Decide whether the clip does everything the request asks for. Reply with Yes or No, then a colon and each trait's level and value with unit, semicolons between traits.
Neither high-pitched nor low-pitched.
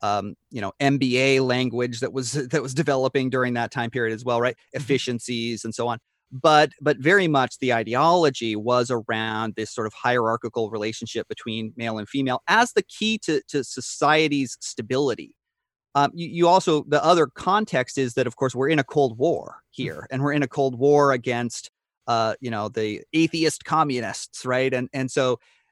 No: low, 130 Hz